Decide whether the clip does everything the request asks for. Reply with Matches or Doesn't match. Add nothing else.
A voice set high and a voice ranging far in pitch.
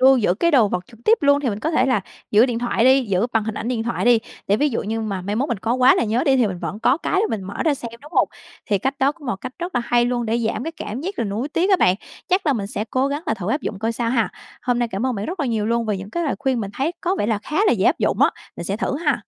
Doesn't match